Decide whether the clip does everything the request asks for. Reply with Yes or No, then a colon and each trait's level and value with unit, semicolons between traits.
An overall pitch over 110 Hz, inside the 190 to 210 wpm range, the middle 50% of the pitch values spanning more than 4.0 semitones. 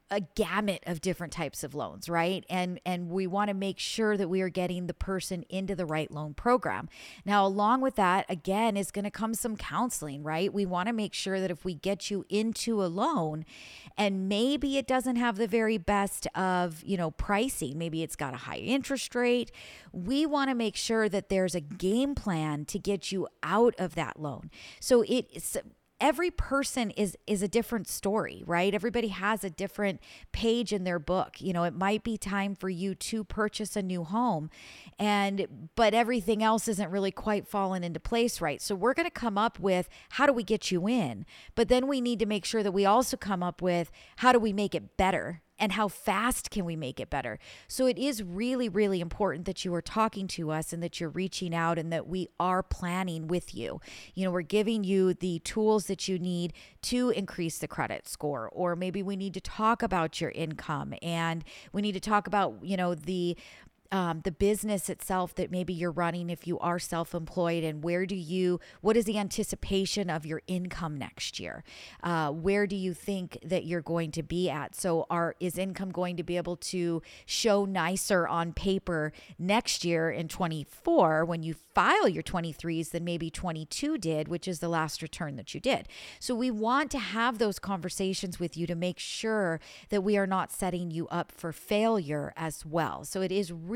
No: high, 190 Hz; fast, 205 wpm; average, 3.7 semitones